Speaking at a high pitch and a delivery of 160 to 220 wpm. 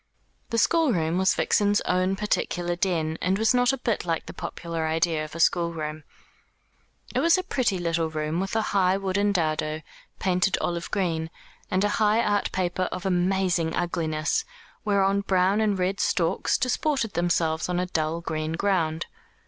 No: medium, 180 Hz; average, 165 wpm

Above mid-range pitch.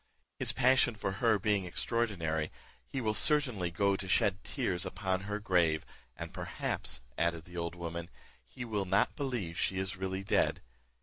No: very low, 95 Hz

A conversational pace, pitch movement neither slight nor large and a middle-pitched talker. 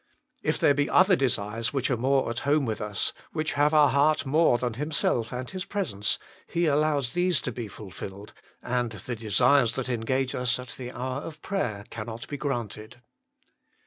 No: average, 180 wpm; average, 4.2 semitones; low, 130 Hz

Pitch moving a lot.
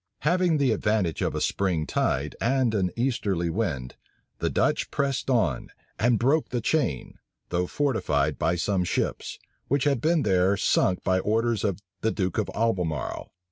Yes: wide, 6.2 semitones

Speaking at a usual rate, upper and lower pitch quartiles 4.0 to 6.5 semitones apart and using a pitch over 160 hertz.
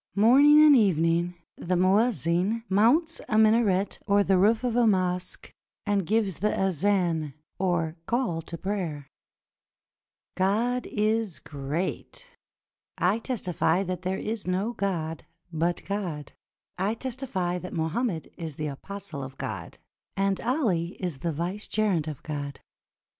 No: slow, 130 wpm; average, 4.5 semitones; high, 190 Hz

